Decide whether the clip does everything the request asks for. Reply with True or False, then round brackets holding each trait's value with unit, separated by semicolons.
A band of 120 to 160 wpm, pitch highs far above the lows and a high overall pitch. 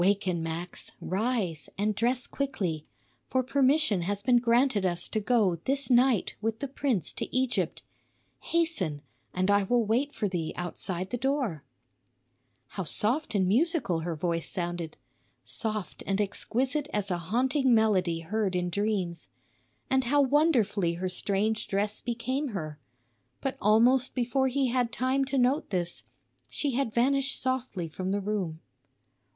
True (145 wpm; 6.0 semitones; 215 Hz)